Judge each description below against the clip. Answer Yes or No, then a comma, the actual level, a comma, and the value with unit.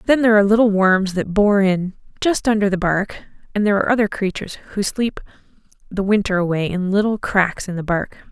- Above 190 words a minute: Yes, average, 200 wpm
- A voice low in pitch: No, high, 200 Hz